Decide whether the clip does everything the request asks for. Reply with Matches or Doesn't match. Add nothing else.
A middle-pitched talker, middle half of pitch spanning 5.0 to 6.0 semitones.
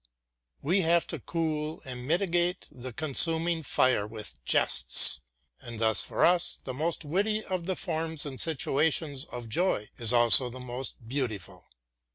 Matches